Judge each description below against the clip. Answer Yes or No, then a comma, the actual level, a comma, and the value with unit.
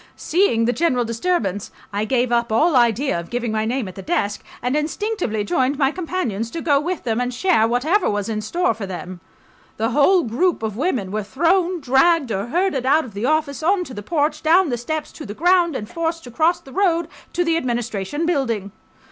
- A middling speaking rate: No, fast, 210 wpm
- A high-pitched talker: Yes, very high, 265 Hz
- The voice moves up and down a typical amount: No, wide, 7.0 semitones